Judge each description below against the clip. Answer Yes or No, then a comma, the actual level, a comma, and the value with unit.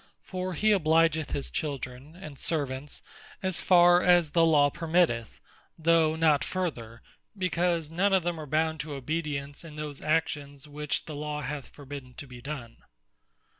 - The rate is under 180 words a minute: Yes, average, 155 wpm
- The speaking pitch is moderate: Yes, medium, 155 Hz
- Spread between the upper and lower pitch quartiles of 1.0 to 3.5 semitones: Yes, average, 2.8 semitones